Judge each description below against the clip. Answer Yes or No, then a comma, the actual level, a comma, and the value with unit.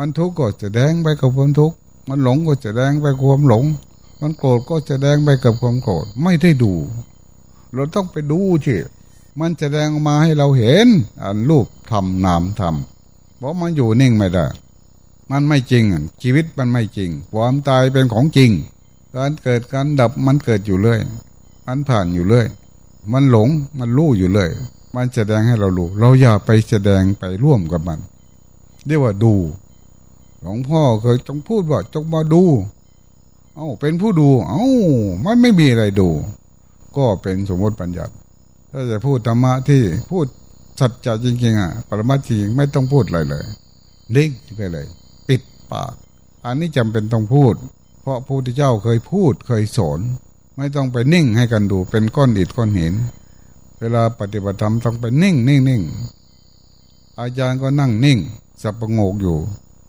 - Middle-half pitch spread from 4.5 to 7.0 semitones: Yes, average, 5.2 semitones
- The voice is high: No, low, 125 Hz